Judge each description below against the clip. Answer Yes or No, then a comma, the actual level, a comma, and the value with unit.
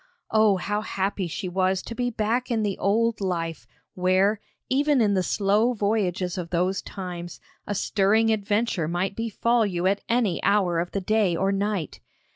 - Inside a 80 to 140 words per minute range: No, average, 170 wpm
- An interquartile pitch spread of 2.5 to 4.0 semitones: Yes, average, 3.1 semitones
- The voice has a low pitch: No, high, 200 Hz